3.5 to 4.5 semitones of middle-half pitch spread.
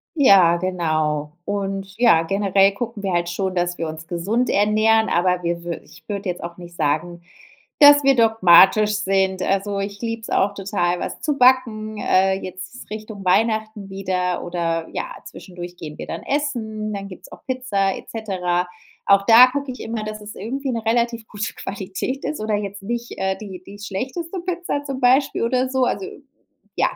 Yes: average, 4.2 semitones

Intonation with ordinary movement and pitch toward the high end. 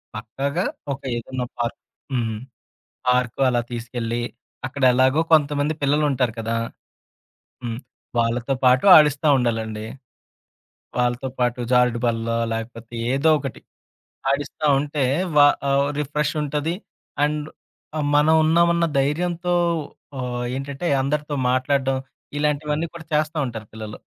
No: average, 3.7 semitones; low, 135 Hz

